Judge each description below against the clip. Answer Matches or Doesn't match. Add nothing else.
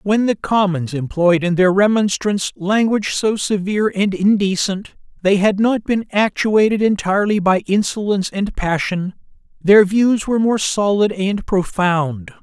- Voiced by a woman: Doesn't match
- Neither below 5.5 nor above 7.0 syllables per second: Doesn't match